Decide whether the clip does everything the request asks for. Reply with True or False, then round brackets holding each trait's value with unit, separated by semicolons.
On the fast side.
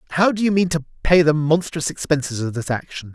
True (230 wpm)